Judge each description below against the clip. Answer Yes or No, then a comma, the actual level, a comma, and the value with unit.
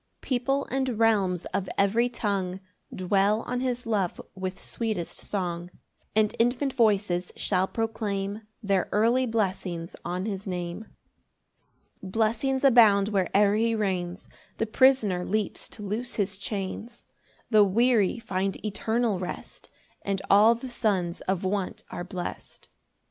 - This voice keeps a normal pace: No, slow, 130 wpm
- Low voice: No, high, 205 Hz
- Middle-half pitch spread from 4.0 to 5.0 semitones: No, average, 3.4 semitones